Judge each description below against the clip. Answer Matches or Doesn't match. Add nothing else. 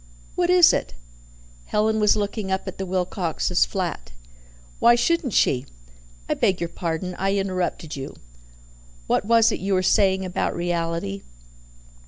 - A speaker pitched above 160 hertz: Matches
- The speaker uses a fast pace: Doesn't match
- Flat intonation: Doesn't match